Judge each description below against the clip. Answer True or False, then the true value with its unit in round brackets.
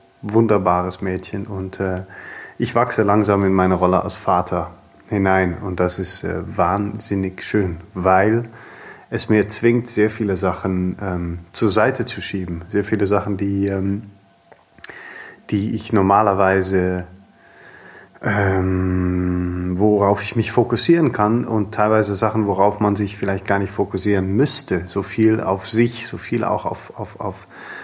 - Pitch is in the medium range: False (100 Hz)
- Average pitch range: False (2.3 semitones)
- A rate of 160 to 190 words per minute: False (140 wpm)